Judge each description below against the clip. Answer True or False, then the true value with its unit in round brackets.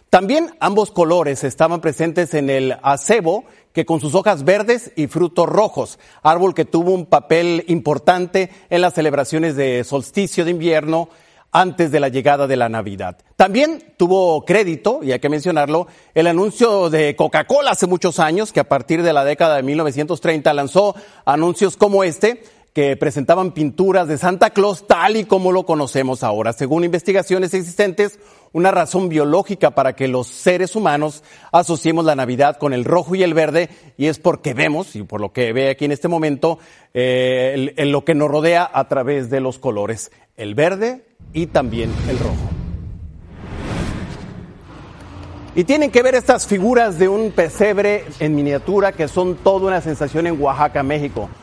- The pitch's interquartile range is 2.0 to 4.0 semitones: False (4.7 semitones)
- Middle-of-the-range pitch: True (165 Hz)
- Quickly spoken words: False (170 wpm)